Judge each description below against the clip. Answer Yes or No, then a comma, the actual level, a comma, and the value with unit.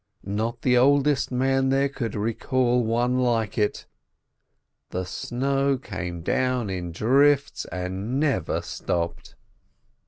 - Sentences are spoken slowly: Yes, slow, 115 wpm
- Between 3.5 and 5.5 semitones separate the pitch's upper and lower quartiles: Yes, average, 4.5 semitones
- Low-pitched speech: Yes, low, 125 Hz